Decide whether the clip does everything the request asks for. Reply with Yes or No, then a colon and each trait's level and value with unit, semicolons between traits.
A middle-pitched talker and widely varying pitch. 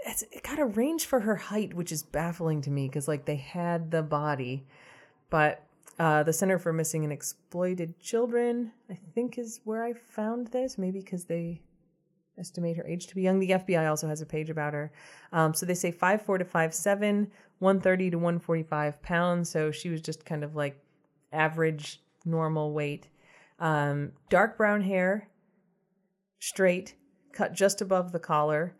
No: medium, 170 Hz; average, 3.9 semitones